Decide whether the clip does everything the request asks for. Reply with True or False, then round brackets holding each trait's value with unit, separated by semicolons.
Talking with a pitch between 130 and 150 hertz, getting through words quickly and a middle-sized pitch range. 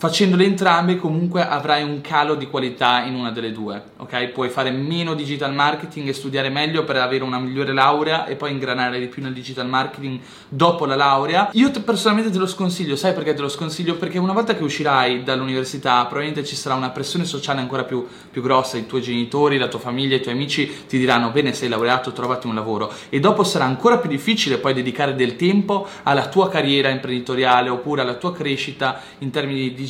True (135 Hz; 205 wpm; 3.3 semitones)